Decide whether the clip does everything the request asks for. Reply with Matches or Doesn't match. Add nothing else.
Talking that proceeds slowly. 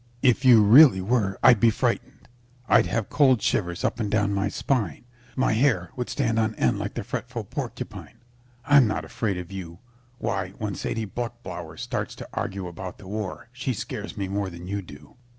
Doesn't match